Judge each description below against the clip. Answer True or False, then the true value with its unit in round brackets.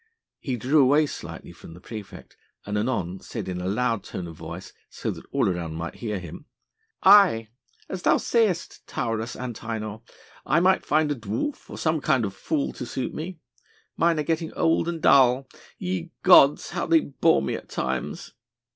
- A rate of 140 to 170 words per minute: False (180 wpm)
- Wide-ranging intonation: True (7.9 semitones)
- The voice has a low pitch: True (125 Hz)